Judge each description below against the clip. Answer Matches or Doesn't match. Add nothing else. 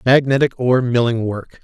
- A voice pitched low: Matches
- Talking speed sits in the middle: Matches